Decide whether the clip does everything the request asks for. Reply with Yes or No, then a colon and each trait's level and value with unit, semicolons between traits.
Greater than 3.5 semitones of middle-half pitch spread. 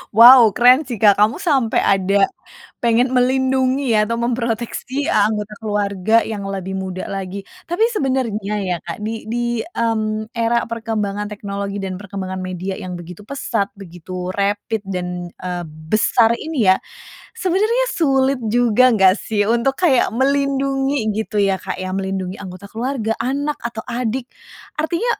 Yes: average, 4.4 semitones